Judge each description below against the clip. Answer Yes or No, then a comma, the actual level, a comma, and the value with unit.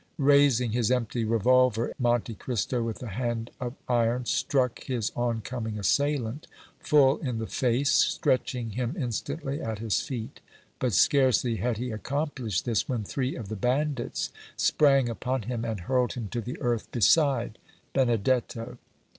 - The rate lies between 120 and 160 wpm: Yes, average, 150 wpm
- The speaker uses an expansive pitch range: No, narrow, 2.4 semitones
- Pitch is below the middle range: Yes, low, 120 Hz